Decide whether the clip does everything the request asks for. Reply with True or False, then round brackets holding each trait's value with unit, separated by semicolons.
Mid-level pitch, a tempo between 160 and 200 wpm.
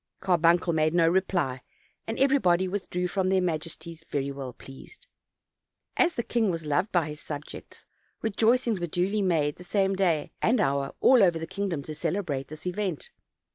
True (175 Hz; 170 wpm)